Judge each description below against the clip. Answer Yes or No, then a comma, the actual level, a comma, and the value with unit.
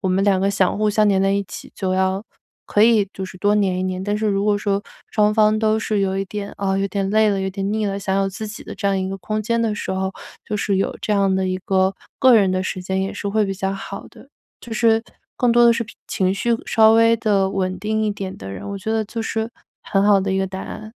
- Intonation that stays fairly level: Yes, narrow, 2.0 semitones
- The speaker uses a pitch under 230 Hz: Yes, high, 200 Hz